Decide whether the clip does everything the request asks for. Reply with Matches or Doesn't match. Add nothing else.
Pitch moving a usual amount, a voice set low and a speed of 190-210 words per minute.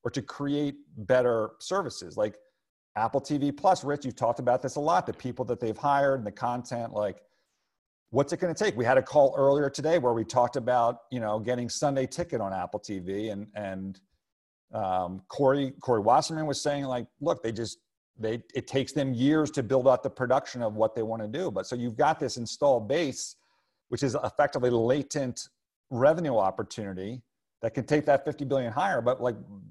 Matches